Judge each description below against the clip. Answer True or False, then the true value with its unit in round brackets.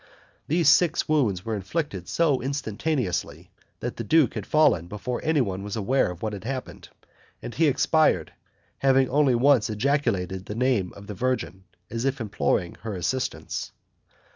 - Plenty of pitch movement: True (6.1 semitones)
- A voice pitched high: False (125 Hz)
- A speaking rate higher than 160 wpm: False (155 wpm)